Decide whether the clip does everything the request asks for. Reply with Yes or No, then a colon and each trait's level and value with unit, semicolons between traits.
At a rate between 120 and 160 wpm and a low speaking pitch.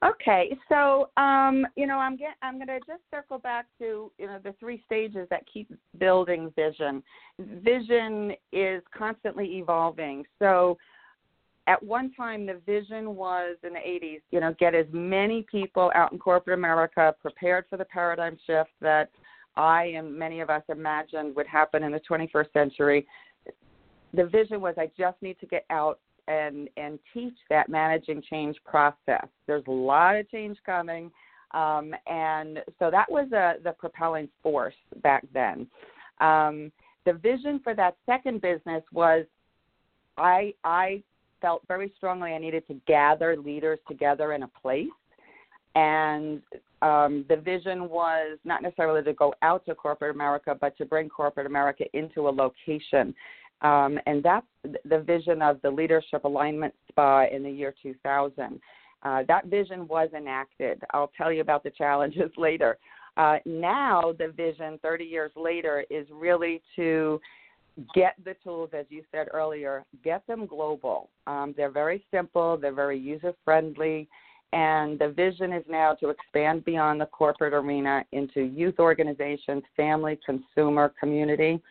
No: average, 155 wpm; medium, 160 Hz